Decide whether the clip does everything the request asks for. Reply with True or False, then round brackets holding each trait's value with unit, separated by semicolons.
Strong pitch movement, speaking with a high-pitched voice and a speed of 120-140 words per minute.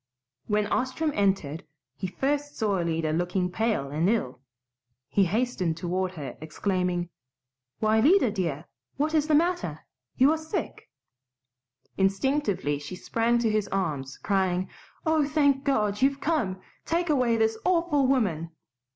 True (7.7 semitones; 210 Hz; 135 wpm)